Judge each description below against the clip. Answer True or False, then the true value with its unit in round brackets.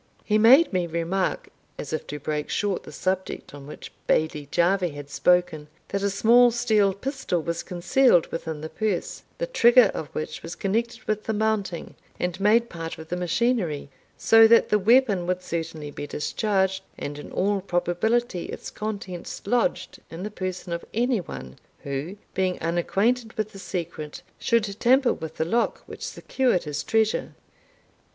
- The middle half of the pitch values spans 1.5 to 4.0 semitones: False (5.0 semitones)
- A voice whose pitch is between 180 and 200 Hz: True (190 Hz)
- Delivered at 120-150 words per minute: False (165 wpm)